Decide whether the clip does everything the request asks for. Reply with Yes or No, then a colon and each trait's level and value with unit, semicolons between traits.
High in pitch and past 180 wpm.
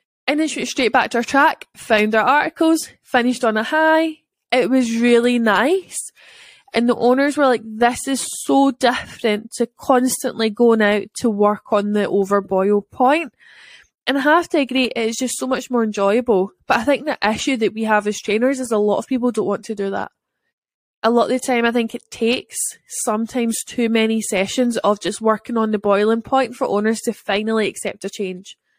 Yes: high, 235 Hz; average, 200 wpm